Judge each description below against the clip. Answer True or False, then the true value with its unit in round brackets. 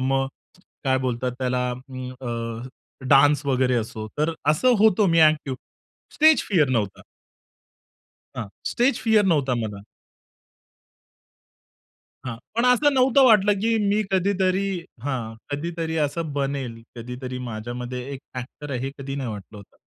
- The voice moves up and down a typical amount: False (7.0 semitones)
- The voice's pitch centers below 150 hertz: True (135 Hz)